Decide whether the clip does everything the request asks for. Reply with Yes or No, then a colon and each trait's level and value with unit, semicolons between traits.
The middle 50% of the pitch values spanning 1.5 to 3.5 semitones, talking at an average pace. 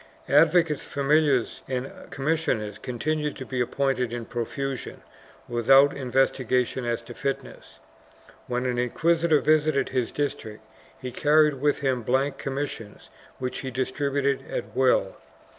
No: average, 2.8 semitones; slow, 130 wpm